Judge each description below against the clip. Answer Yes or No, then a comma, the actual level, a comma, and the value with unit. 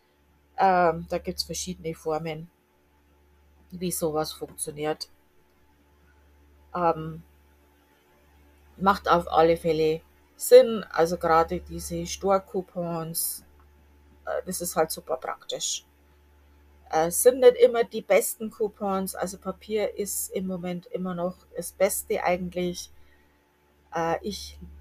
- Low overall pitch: No, medium, 160 Hz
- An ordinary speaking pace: No, slow, 110 wpm